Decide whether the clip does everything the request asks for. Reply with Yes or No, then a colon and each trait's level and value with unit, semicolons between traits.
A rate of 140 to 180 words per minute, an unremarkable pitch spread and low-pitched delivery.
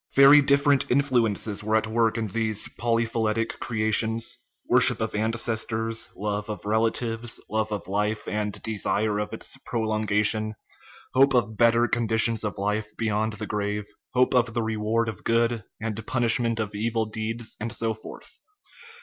No: average, 155 wpm; narrow, 1.4 semitones; low, 110 Hz